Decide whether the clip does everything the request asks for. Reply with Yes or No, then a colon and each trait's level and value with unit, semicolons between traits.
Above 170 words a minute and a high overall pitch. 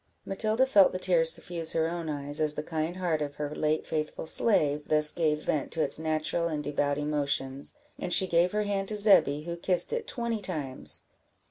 No: average, 200 wpm; medium, 160 Hz